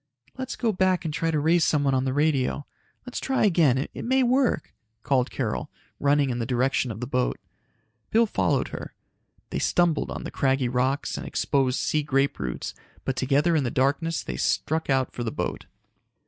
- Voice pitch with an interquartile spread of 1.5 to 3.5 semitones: No, average, 4.1 semitones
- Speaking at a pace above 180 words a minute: Yes, average, 190 wpm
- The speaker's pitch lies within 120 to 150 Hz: Yes, medium, 140 Hz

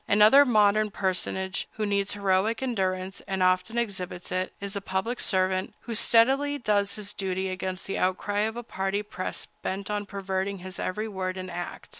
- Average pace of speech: Yes, average, 175 wpm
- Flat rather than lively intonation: Yes, narrow, 2.2 semitones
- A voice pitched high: Yes, high, 195 Hz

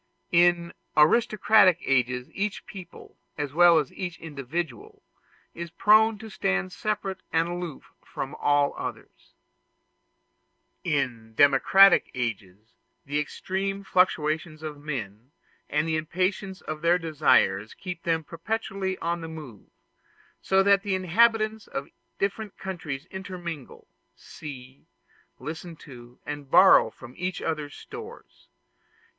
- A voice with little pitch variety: No, average, 5.0 semitones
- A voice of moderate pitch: Yes, medium, 165 Hz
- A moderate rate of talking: No, slow, 115 wpm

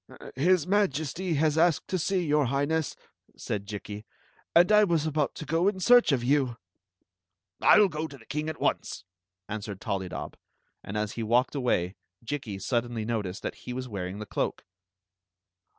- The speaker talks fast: No, average, 175 wpm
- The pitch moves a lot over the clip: Yes, wide, 7.1 semitones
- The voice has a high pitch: No, low, 135 Hz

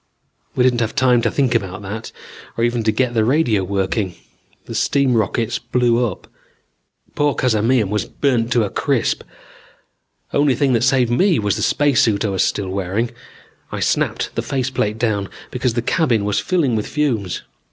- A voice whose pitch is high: No, low, 115 Hz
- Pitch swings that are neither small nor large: Yes, average, 3.5 semitones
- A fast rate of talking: No, average, 175 wpm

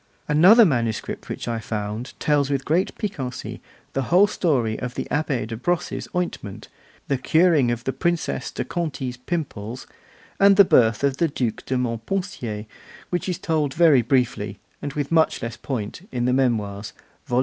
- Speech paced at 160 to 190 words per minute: Yes, average, 165 wpm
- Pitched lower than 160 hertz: Yes, low, 135 Hz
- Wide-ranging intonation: Yes, wide, 5.9 semitones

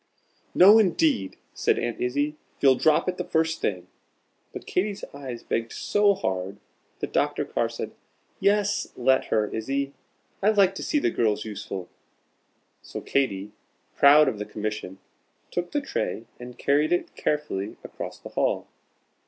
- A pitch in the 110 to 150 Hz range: Yes, medium, 140 Hz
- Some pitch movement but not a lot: No, wide, 8.8 semitones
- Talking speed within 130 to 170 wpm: Yes, average, 150 wpm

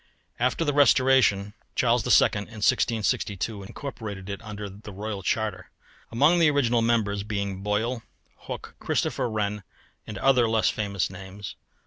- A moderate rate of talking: No, slow, 130 wpm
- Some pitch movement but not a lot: Yes, average, 3.0 semitones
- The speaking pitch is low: Yes, low, 110 Hz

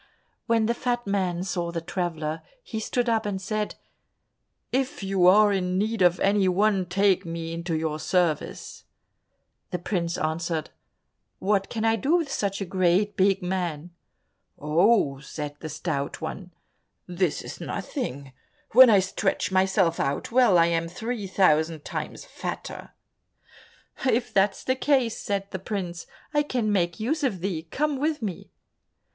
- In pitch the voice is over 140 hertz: Yes, high, 190 Hz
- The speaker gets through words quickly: No, average, 150 wpm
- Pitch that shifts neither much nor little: Yes, average, 4.2 semitones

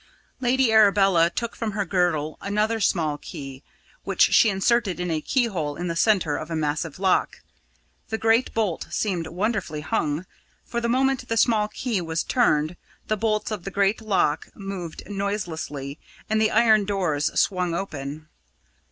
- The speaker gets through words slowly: No, average, 160 wpm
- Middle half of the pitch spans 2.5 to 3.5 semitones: No, average, 5.2 semitones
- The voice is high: Yes, high, 195 Hz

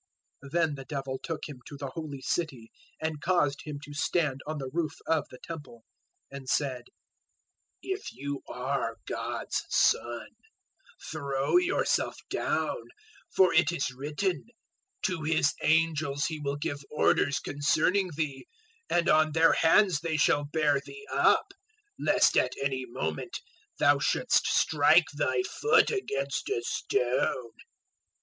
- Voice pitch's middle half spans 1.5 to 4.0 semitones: Yes, average, 3.0 semitones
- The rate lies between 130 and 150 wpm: Yes, average, 140 wpm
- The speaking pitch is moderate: Yes, medium, 145 Hz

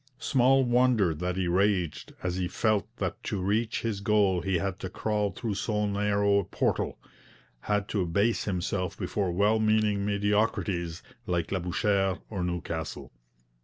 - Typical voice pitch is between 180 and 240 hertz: No, low, 100 Hz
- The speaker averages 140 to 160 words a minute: Yes, average, 150 wpm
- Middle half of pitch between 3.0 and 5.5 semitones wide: No, narrow, 2.6 semitones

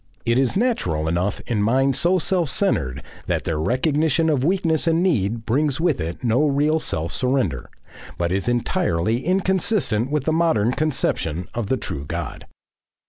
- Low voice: Yes, low, 130 Hz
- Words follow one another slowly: No, average, 165 wpm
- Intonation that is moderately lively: No, wide, 7.7 semitones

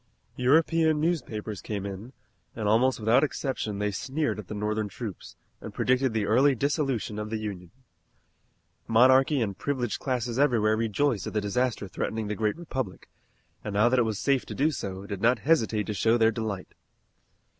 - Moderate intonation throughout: Yes, average, 3.8 semitones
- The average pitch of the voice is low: Yes, low, 115 Hz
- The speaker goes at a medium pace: Yes, average, 175 wpm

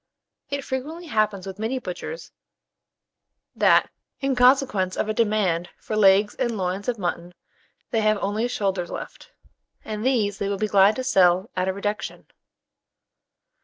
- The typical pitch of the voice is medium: No, high, 210 Hz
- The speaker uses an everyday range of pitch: Yes, average, 3.8 semitones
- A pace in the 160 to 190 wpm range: No, average, 150 wpm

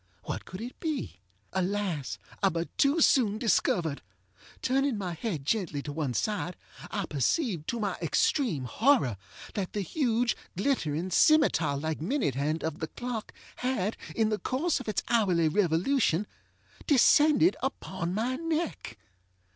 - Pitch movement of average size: No, wide, 7.9 semitones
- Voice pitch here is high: Yes, high, 205 Hz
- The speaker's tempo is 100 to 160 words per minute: Yes, average, 140 wpm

